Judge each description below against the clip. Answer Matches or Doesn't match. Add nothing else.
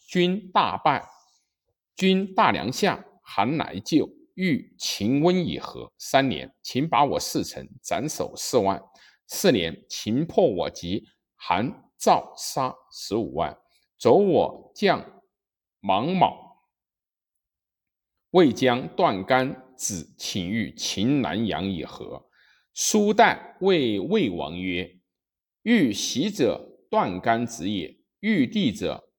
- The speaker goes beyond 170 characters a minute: Doesn't match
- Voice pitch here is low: Matches